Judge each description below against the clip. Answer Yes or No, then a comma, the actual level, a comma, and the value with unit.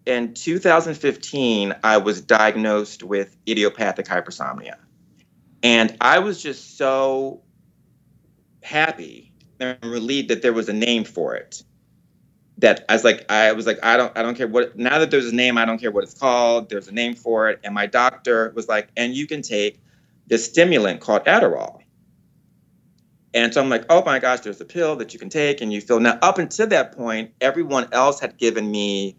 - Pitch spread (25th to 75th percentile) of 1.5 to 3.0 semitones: No, average, 3.6 semitones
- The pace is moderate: Yes, average, 190 wpm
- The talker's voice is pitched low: Yes, low, 120 Hz